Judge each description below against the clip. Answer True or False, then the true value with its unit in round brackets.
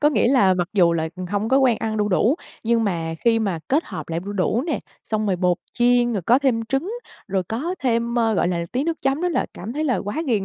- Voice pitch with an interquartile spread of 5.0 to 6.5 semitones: True (5.5 semitones)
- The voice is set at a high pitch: True (225 Hz)